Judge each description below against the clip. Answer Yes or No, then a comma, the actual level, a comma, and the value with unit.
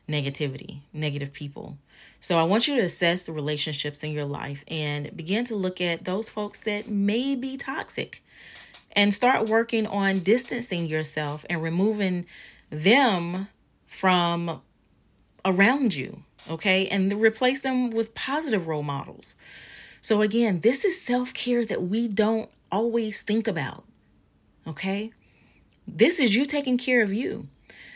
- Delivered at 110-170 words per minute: Yes, average, 140 wpm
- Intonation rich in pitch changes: Yes, wide, 6.5 semitones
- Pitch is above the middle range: Yes, high, 200 Hz